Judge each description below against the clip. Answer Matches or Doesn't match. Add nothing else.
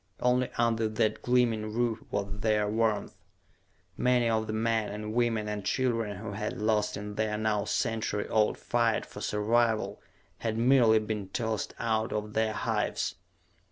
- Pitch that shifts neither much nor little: Doesn't match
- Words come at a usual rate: Matches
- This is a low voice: Matches